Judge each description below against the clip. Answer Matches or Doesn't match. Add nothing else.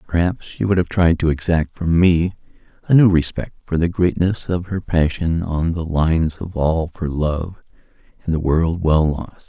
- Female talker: Doesn't match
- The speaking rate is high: Doesn't match